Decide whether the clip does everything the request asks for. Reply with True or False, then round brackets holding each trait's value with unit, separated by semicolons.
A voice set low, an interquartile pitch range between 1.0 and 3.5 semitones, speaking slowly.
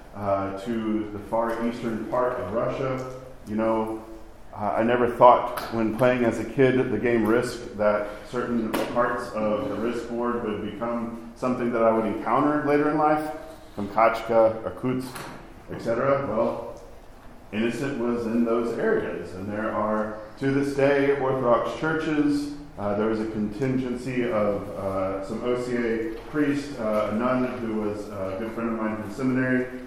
False (115 Hz; 2.8 semitones; 160 wpm)